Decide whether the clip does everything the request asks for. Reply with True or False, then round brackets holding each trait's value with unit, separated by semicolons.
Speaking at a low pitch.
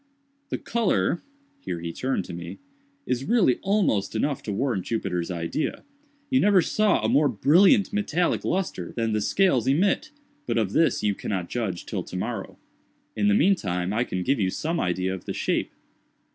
True (130 Hz)